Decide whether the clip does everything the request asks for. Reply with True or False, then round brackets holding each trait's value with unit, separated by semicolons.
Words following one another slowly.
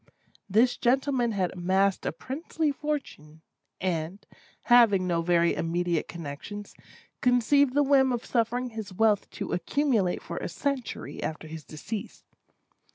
True (130 wpm)